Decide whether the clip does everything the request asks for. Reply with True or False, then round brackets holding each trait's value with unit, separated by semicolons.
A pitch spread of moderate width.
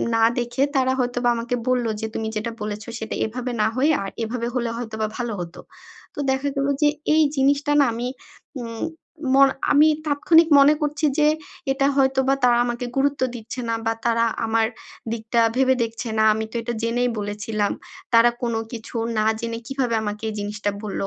True (3.0 semitones)